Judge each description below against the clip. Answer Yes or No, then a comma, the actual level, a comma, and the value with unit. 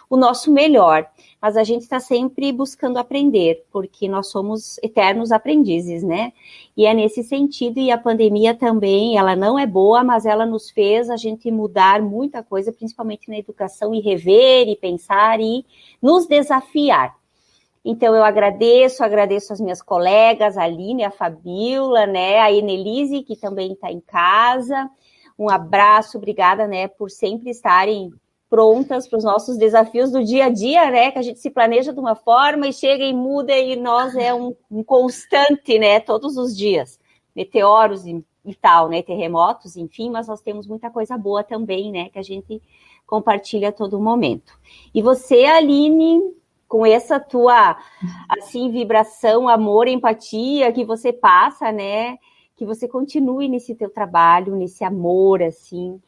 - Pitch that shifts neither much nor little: Yes, average, 3.7 semitones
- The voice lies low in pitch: No, high, 225 Hz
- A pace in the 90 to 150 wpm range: No, average, 160 wpm